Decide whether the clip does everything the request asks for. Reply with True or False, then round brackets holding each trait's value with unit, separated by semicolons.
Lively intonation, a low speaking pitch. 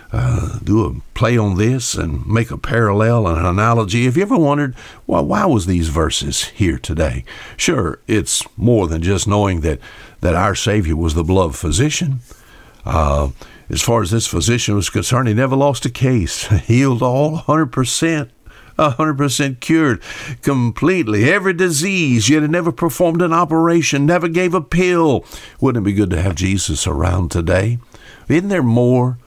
True (6.5 semitones; 115 Hz)